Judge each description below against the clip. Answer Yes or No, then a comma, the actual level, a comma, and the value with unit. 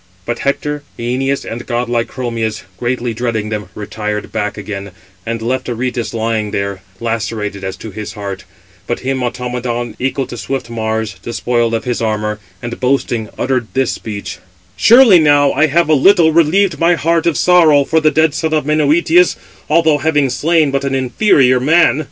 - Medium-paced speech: Yes, average, 170 wpm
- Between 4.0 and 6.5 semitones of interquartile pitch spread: Yes, average, 5.1 semitones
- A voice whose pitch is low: Yes, low, 125 Hz